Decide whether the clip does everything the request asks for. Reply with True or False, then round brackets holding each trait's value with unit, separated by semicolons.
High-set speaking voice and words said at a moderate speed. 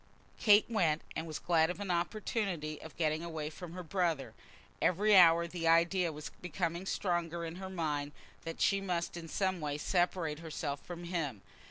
False (170 Hz; 175 wpm)